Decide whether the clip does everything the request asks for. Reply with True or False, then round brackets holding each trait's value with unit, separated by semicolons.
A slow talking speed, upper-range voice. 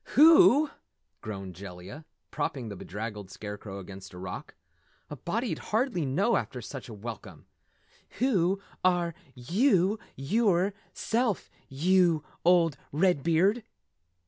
False (105 wpm; 165 Hz)